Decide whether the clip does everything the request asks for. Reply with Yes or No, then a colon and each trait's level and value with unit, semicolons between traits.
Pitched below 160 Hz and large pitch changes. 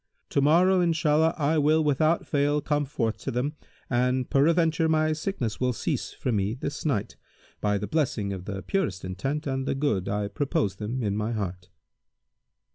Yes: low, 135 Hz; wide, 6.7 semitones